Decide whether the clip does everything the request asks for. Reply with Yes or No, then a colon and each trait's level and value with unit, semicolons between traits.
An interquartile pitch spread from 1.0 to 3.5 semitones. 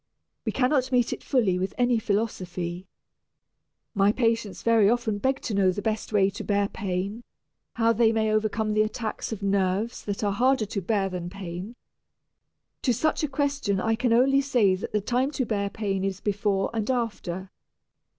Yes: average, 3.2 semitones